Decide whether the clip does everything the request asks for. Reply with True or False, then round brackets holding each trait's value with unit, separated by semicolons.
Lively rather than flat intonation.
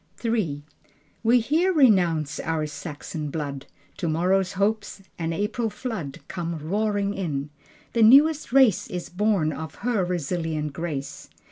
True (5.9 semitones)